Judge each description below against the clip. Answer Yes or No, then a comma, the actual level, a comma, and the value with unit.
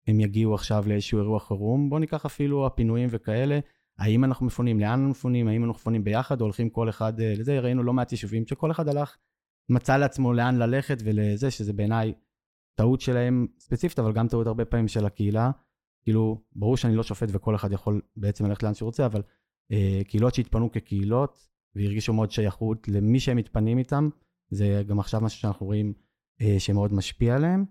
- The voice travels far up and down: No, average, 3.1 semitones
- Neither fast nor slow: No, fast, 180 wpm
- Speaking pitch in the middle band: No, low, 115 Hz